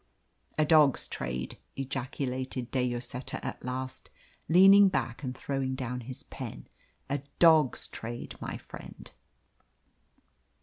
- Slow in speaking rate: Yes, slow, 115 wpm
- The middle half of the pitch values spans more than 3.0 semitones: No, narrow, 2.5 semitones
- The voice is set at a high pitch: No, low, 130 Hz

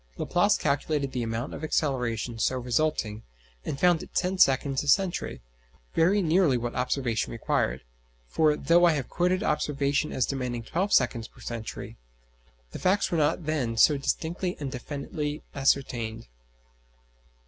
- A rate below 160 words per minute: Yes, average, 145 wpm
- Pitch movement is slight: No, average, 4.7 semitones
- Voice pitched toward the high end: No, medium, 140 Hz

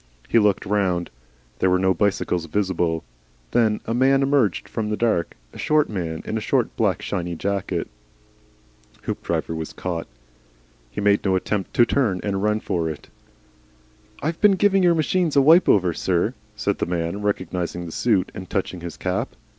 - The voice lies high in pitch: No, low, 100 Hz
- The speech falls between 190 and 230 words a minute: No, average, 170 wpm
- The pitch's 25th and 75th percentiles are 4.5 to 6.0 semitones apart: Yes, average, 4.8 semitones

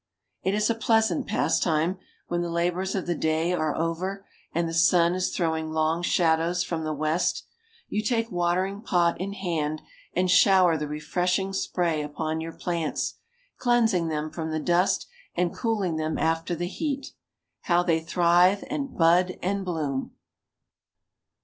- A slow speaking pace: No, average, 155 wpm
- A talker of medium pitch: Yes, medium, 175 Hz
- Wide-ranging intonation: No, average, 2.8 semitones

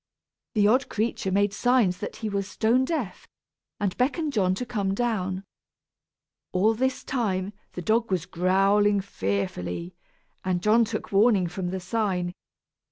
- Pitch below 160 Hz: No, high, 200 Hz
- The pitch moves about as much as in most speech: Yes, average, 3.6 semitones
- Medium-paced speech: Yes, average, 145 wpm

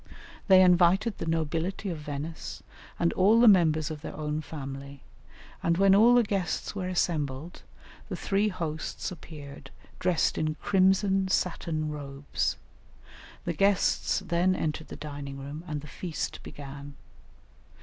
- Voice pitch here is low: No, medium, 165 Hz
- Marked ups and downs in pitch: No, average, 4.0 semitones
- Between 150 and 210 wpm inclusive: No, average, 140 wpm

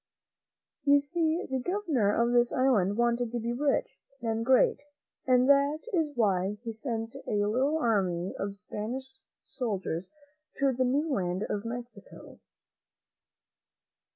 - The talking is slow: Yes, slow, 130 wpm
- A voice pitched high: Yes, high, 240 Hz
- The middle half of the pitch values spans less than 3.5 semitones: No, average, 4.8 semitones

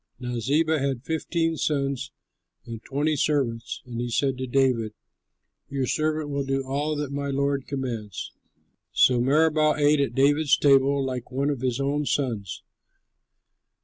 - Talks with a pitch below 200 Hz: Yes, medium, 140 Hz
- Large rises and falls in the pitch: No, narrow, 2.4 semitones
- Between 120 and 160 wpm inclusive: Yes, average, 145 wpm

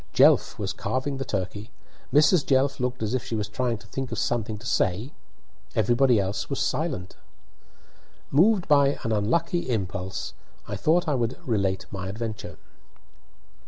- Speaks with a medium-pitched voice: No, low, 115 Hz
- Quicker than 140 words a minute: Yes, average, 155 wpm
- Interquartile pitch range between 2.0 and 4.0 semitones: No, average, 4.9 semitones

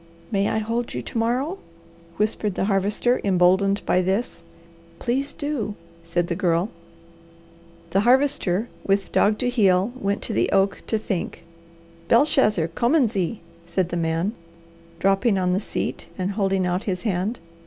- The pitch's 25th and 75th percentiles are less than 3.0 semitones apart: No, average, 4.0 semitones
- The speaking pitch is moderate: No, high, 200 Hz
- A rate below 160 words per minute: Yes, average, 150 wpm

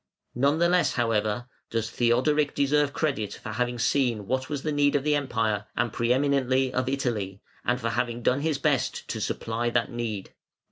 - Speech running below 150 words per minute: No, average, 180 wpm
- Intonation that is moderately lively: Yes, average, 3.5 semitones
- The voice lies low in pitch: Yes, low, 125 Hz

